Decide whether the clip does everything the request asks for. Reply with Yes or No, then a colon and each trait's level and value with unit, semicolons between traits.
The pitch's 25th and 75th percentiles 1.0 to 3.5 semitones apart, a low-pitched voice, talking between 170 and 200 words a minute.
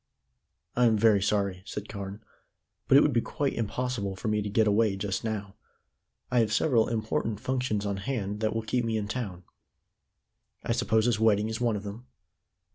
Yes: narrow, 2.5 semitones; low, 110 Hz; average, 190 wpm